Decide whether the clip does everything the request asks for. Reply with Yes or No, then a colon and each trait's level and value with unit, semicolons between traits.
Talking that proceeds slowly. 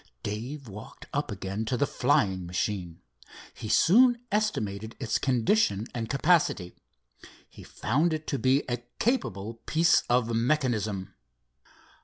Yes: slow, 125 wpm